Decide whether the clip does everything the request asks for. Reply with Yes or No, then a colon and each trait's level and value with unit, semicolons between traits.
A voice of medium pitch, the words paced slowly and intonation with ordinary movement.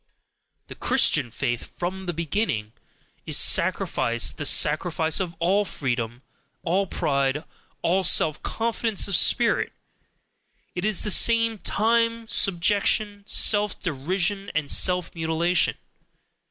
Yes: medium, 180 Hz; slow, 115 wpm; average, 5.0 semitones